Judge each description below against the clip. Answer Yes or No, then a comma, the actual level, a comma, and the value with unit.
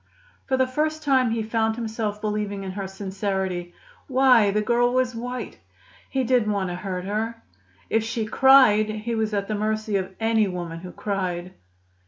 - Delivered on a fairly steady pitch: No, average, 3.3 semitones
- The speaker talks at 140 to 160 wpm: No, average, 175 wpm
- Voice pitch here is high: Yes, high, 215 Hz